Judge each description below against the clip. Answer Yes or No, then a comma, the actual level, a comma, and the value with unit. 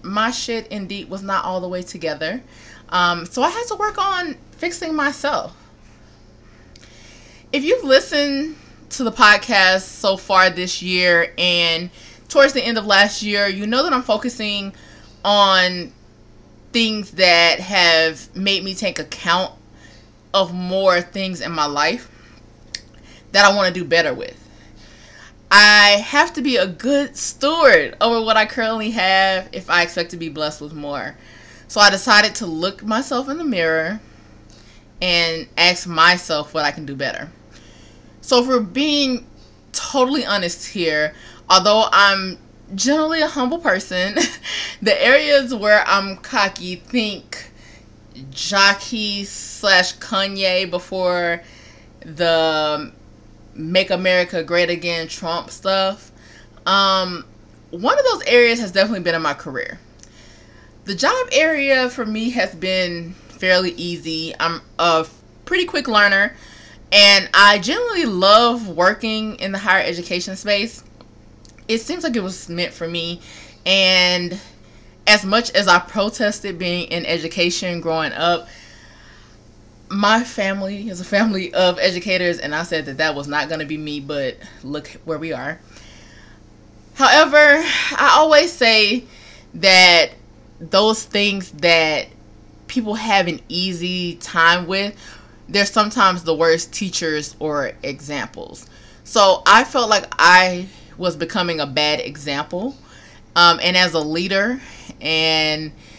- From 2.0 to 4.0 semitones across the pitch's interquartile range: No, average, 5.0 semitones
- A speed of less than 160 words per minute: Yes, slow, 135 wpm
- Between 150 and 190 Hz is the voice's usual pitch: Yes, medium, 185 Hz